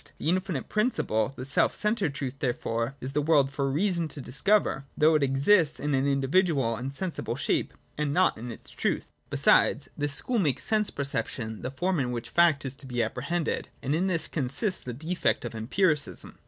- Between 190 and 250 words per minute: Yes, average, 195 wpm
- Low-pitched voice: No, medium, 145 Hz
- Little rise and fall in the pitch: No, average, 5.0 semitones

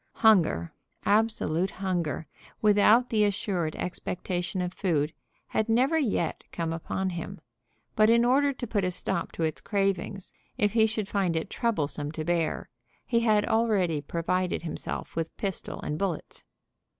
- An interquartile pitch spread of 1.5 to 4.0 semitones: No, average, 4.6 semitones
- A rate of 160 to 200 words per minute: No, average, 150 wpm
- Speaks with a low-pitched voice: No, high, 190 Hz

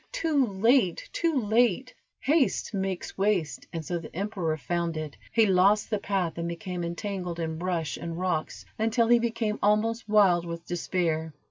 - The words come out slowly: No, average, 160 wpm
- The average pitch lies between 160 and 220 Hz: Yes, high, 190 Hz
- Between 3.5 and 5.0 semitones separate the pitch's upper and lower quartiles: Yes, average, 4.7 semitones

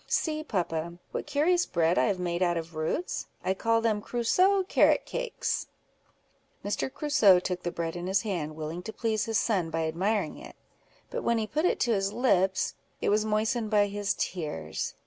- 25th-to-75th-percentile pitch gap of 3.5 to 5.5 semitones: Yes, average, 5.2 semitones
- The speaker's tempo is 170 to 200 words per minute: Yes, average, 185 wpm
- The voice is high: Yes, high, 205 Hz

